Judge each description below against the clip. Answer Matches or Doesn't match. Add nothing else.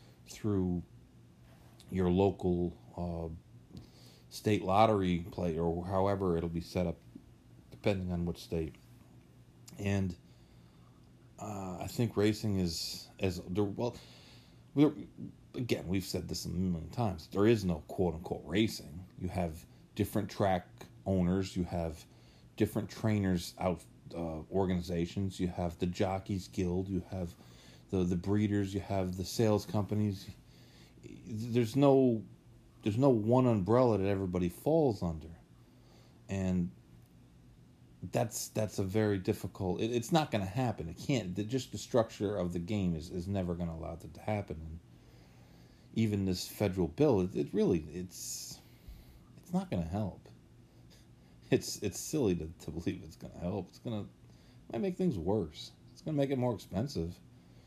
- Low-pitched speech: Matches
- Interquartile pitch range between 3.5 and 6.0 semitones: Matches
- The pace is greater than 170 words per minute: Doesn't match